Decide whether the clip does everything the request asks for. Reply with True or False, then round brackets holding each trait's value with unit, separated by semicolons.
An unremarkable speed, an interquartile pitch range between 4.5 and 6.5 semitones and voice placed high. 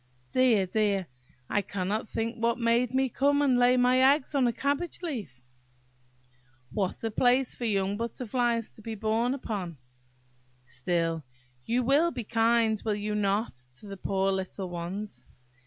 False (155 wpm; 4.0 semitones; 225 Hz)